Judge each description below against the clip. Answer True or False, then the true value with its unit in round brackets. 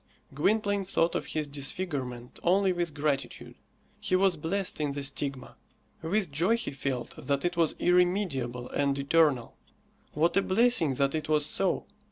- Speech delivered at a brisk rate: False (155 wpm)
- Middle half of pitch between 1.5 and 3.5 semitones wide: False (4.9 semitones)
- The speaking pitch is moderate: True (155 Hz)